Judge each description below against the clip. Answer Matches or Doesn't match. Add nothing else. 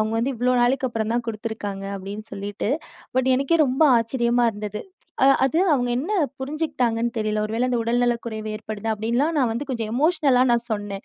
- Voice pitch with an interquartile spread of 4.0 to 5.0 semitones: Doesn't match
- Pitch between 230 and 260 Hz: Matches